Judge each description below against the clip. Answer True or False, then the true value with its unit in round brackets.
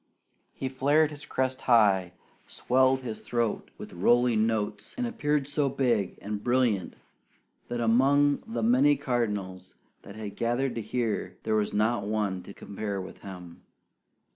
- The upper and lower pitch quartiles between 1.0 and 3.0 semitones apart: False (4.2 semitones)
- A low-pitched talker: True (115 Hz)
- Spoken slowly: False (145 wpm)